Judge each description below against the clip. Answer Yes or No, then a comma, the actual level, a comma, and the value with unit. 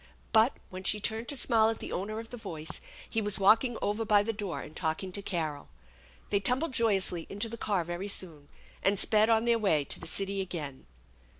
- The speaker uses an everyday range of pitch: Yes, average, 3.7 semitones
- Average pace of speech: No, fast, 210 wpm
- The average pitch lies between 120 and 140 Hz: No, high, 205 Hz